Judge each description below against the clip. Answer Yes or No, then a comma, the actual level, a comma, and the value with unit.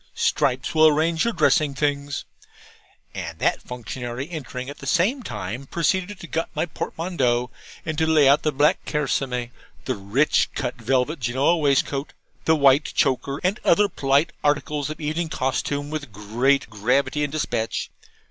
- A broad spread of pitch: No, average, 3.6 semitones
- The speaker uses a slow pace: No, average, 155 wpm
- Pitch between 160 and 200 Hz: No, medium, 145 Hz